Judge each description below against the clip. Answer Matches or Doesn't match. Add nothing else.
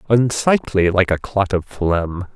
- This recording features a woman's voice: Doesn't match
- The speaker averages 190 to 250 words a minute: Doesn't match